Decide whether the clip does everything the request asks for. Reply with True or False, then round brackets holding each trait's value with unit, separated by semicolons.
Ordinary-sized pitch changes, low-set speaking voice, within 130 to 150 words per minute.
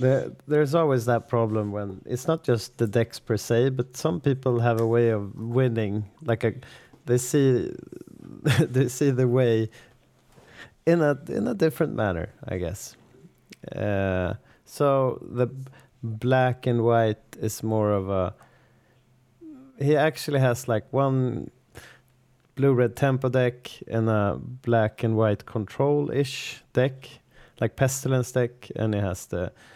True (3.4 semitones; 125 Hz; 145 wpm)